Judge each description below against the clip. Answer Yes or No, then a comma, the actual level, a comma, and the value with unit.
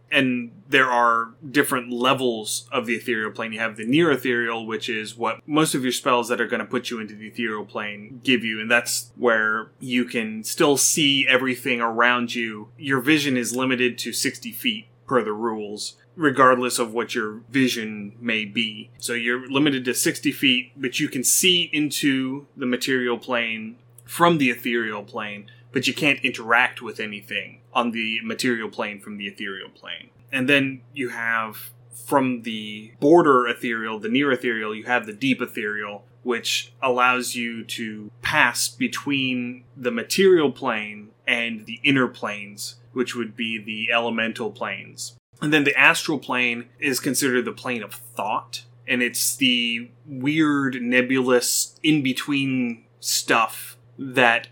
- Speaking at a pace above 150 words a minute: Yes, average, 160 wpm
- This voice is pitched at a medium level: No, low, 120 Hz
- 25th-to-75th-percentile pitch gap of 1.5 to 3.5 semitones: Yes, narrow, 2.4 semitones